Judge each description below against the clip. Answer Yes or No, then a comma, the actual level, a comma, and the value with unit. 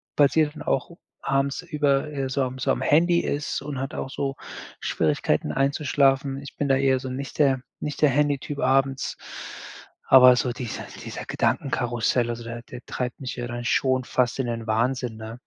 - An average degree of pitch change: No, narrow, 2.3 semitones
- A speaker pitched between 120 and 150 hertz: Yes, low, 135 Hz